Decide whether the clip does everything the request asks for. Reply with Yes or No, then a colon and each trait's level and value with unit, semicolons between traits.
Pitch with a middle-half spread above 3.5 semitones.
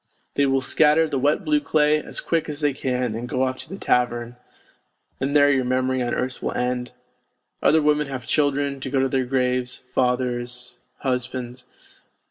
No: narrow, 2.4 semitones